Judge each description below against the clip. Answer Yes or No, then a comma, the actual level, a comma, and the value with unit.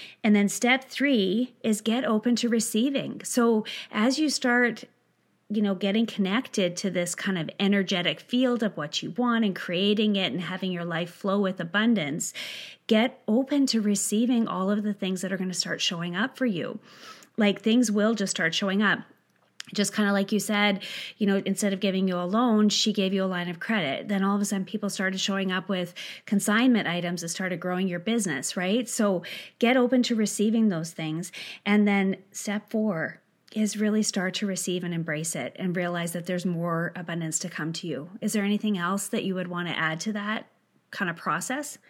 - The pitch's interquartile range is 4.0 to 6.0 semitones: No, average, 3.3 semitones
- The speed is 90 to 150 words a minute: No, fast, 205 wpm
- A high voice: Yes, high, 200 Hz